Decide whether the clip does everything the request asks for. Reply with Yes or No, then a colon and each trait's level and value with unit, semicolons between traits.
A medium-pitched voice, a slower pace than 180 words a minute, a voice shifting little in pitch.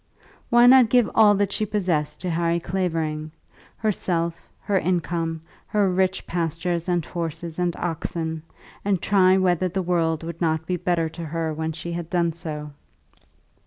Yes: medium, 170 Hz; average, 160 wpm; narrow, 2.3 semitones